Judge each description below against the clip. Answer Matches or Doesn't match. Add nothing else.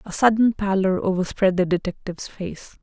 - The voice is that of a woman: Matches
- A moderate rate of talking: Matches